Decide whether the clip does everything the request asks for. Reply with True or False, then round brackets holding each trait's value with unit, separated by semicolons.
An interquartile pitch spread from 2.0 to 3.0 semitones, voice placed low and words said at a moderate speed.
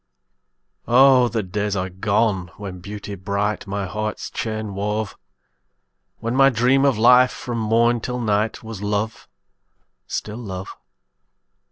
False (2.7 semitones; 110 Hz; 130 wpm)